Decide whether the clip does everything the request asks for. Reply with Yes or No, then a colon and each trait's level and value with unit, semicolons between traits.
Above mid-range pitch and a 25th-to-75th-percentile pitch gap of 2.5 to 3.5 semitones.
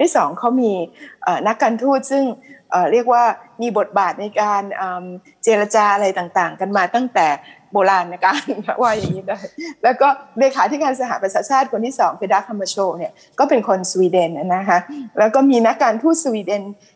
No: high, 215 Hz; average, 4.9 semitones